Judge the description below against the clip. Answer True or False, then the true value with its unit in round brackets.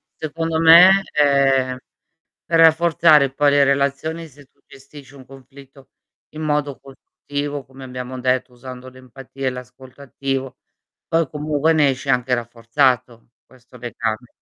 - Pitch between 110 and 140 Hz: True (135 Hz)